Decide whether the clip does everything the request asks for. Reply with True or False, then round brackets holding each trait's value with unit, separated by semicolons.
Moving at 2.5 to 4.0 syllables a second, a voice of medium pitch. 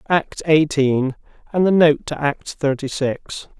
True (3.8 syllables/s; 150 Hz)